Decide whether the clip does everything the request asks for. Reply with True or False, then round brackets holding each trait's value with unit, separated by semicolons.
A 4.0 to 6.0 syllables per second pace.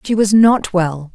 False (3.8 syllables/s)